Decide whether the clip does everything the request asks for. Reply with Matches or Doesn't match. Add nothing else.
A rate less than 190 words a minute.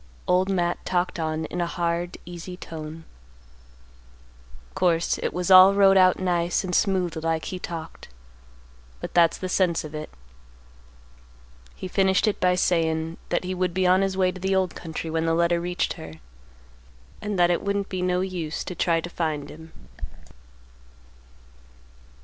Matches